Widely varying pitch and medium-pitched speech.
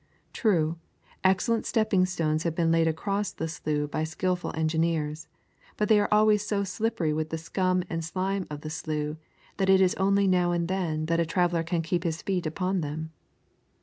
No: average, 3.2 semitones; medium, 170 Hz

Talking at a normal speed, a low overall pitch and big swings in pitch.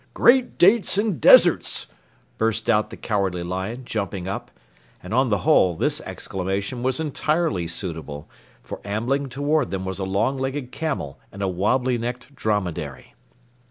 Yes: average, 150 wpm; low, 110 Hz; wide, 6.1 semitones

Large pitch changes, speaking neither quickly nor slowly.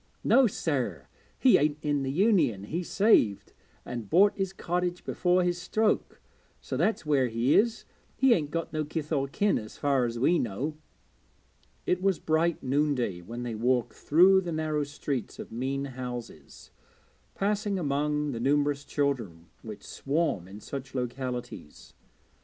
Yes: wide, 6.0 semitones; average, 150 wpm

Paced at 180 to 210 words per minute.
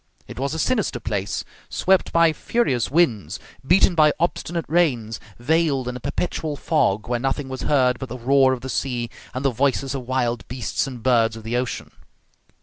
Yes: average, 185 wpm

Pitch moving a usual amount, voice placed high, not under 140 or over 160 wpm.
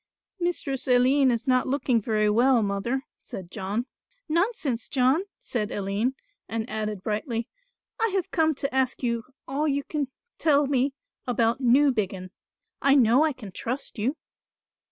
Yes: average, 4.1 semitones; very high, 250 Hz; average, 145 wpm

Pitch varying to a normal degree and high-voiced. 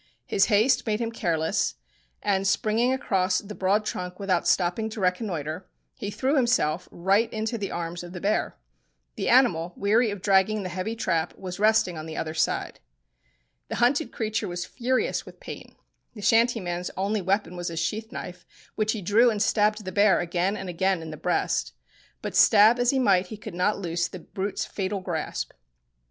Yes: average, 3.6 semitones; high, 195 Hz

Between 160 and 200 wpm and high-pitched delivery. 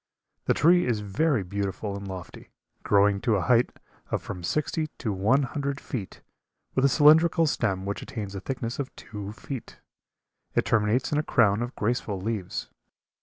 No: average, 170 wpm; low, 115 Hz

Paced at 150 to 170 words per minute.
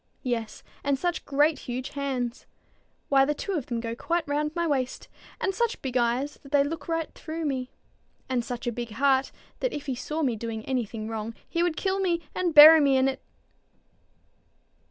No: average, 195 wpm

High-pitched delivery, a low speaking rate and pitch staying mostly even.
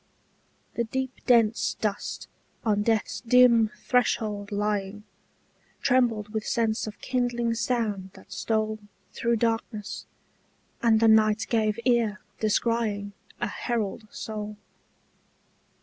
Yes: high, 220 Hz; slow, 105 wpm; narrow, 2.0 semitones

